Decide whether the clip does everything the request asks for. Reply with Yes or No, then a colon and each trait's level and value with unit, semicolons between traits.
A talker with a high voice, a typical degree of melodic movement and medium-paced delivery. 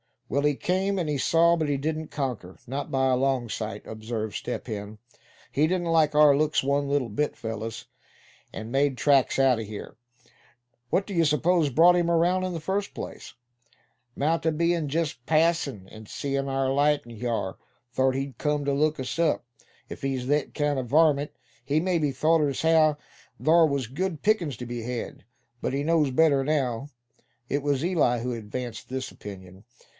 No: medium, 140 Hz; average, 4.3 semitones; average, 185 wpm